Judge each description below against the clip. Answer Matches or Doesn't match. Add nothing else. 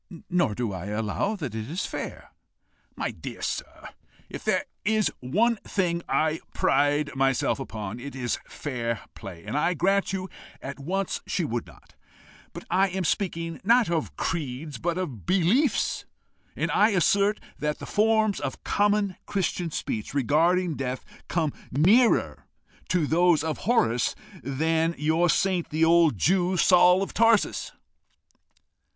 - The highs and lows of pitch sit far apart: Matches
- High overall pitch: Doesn't match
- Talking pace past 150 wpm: Doesn't match